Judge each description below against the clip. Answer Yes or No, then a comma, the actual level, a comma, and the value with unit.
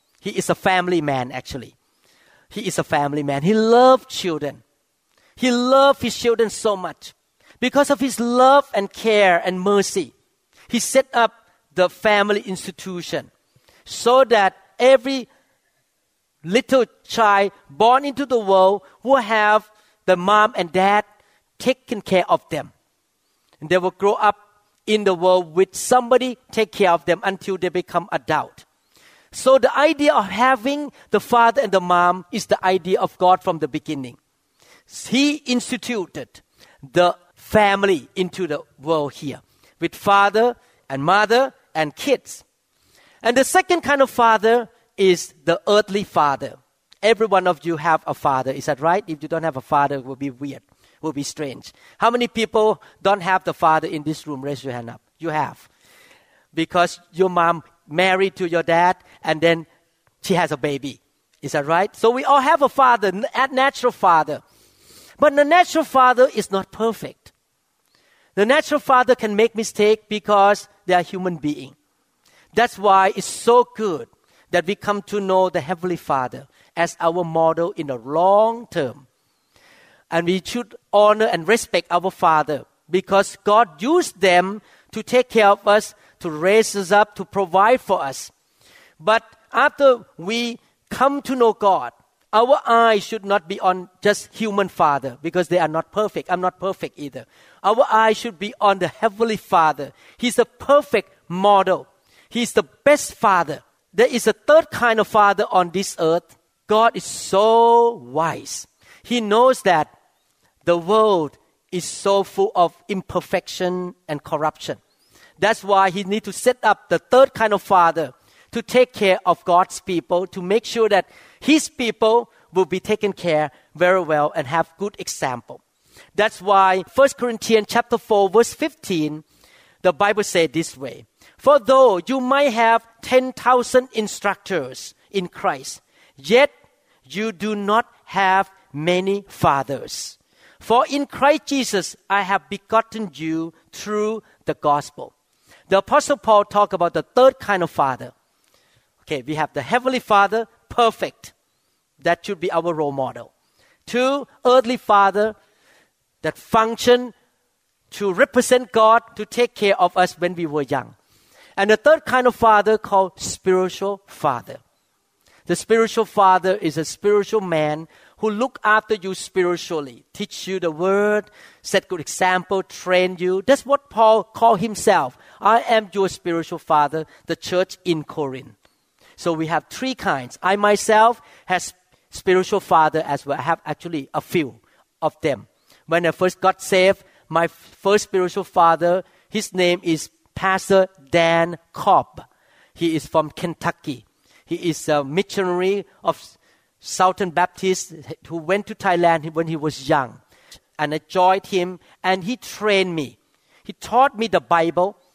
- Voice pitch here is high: Yes, high, 195 Hz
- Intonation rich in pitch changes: No, average, 4.9 semitones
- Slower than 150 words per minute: No, average, 155 wpm